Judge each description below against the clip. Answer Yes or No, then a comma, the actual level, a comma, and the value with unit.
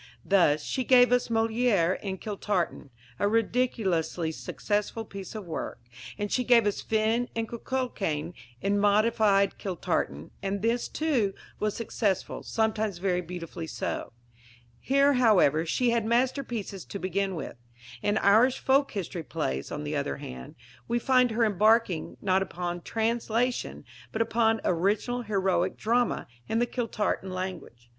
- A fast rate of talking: No, average, 140 wpm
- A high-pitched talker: Yes, high, 210 Hz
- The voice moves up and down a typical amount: Yes, average, 4.1 semitones